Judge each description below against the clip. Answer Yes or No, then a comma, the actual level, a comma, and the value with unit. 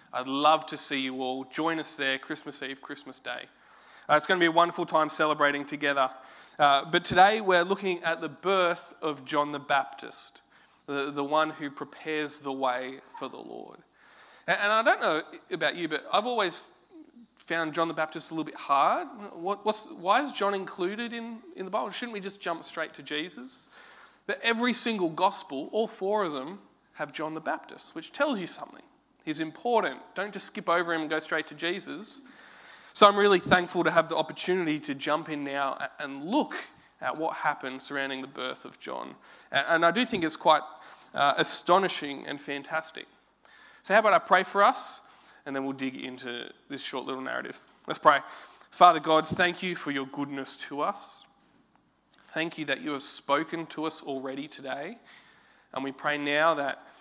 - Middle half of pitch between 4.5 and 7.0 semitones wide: Yes, average, 5.3 semitones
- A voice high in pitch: No, medium, 160 Hz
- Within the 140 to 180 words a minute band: No, average, 190 wpm